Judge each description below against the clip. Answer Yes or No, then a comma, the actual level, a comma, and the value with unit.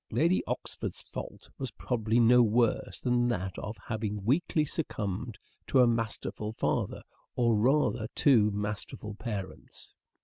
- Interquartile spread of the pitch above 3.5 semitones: No, average, 2.7 semitones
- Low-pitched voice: Yes, low, 115 Hz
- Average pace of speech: No, slow, 130 wpm